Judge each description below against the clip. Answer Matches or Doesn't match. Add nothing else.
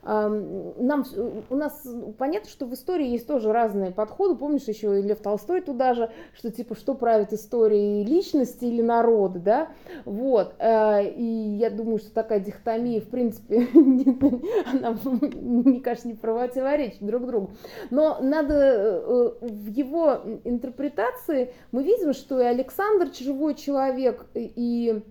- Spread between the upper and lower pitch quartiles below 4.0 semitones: Doesn't match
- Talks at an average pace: Matches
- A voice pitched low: Doesn't match